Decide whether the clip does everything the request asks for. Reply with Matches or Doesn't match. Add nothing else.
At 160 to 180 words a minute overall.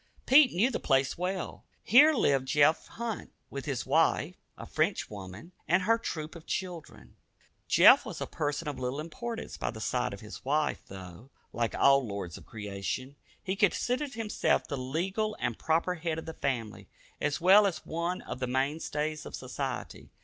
Matches